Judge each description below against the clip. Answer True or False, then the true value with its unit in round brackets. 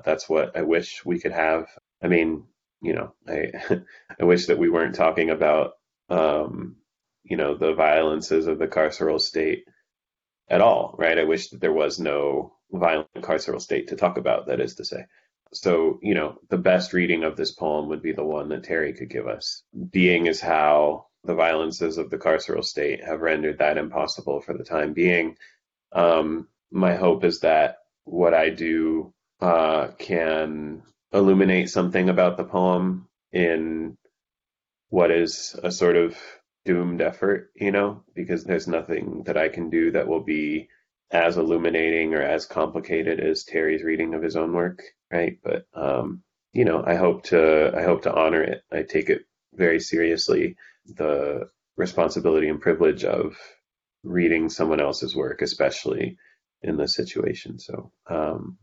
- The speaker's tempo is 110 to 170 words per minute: True (165 wpm)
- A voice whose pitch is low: True (90 Hz)